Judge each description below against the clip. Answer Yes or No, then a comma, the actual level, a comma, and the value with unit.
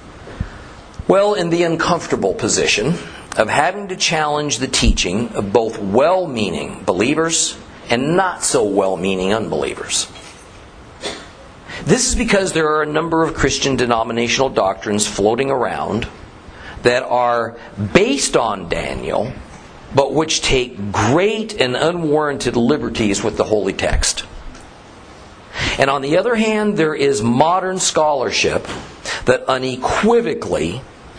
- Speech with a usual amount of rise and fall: No, wide, 6.0 semitones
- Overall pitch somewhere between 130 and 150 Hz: Yes, medium, 140 Hz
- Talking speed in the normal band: No, slow, 120 wpm